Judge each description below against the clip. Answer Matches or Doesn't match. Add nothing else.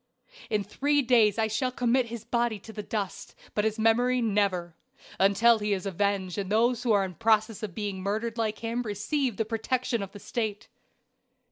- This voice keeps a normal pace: Matches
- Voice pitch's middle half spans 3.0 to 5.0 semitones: Doesn't match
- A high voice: Matches